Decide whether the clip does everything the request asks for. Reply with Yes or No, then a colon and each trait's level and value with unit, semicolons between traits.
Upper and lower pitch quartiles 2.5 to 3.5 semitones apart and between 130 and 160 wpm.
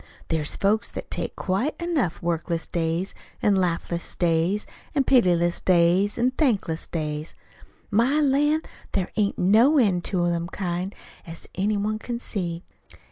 No: average, 5.1 semitones; average, 145 wpm